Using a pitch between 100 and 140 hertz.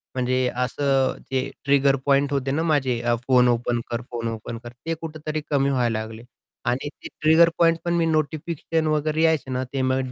Yes: low, 135 Hz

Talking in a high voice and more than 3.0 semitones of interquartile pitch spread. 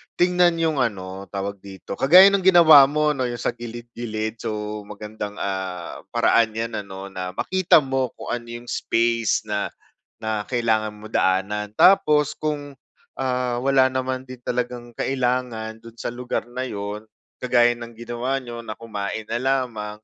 No: low, 120 Hz; average, 3.5 semitones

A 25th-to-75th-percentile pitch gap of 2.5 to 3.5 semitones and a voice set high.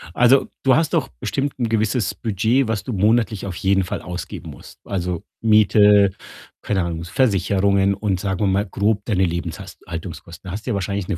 No: average, 2.9 semitones; low, 100 Hz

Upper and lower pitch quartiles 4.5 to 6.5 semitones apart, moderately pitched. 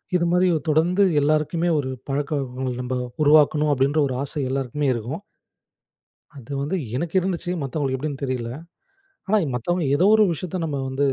No: average, 4.0 semitones; medium, 145 Hz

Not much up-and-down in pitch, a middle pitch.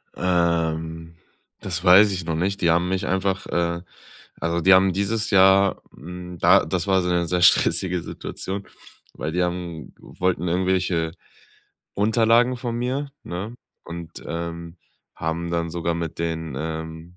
No: narrow, 2.3 semitones; very low, 90 Hz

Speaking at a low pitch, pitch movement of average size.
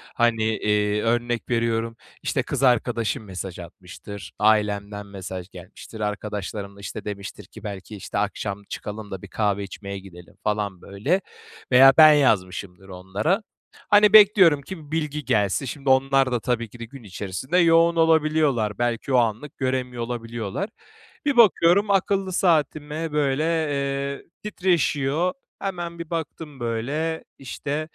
No: low, 120 Hz; wide, 6.9 semitones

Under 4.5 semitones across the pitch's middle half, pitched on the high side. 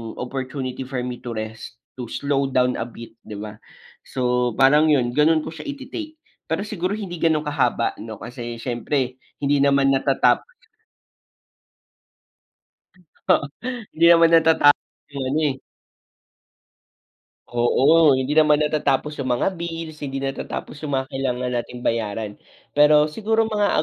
No: average, 4.0 semitones; medium, 140 Hz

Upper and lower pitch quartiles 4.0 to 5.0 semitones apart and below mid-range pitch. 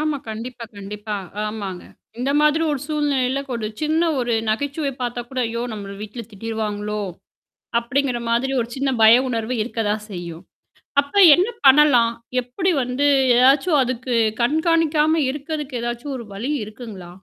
No: average, 4.6 semitones; high, 245 Hz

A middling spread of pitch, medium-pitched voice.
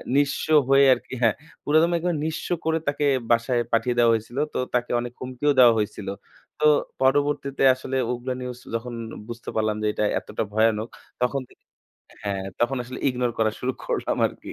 No: average, 3.2 semitones; low, 125 Hz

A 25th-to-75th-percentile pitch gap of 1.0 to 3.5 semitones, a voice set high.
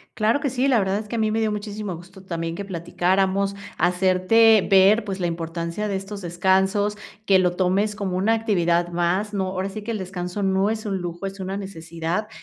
Yes: average, 2.8 semitones; high, 195 Hz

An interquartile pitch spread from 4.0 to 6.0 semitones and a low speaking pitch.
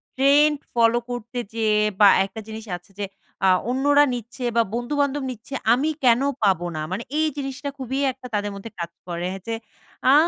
No: average, 4.3 semitones; high, 240 Hz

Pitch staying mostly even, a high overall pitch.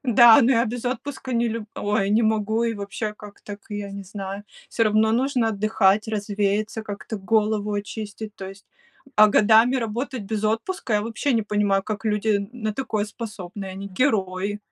Yes: narrow, 2.0 semitones; high, 215 Hz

